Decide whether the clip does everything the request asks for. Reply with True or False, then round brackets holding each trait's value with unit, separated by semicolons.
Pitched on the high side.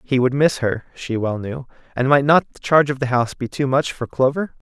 False (135 Hz)